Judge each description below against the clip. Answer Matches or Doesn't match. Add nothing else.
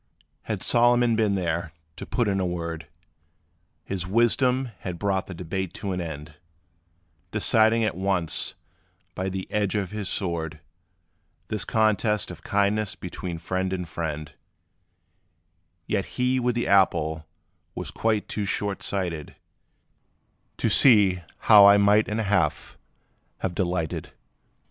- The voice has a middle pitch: Doesn't match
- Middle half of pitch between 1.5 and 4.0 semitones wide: Matches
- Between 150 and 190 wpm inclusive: Doesn't match